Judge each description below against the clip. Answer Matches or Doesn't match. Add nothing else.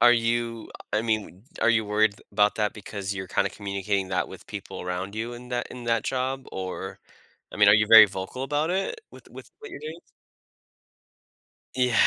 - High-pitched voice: Doesn't match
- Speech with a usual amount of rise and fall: Matches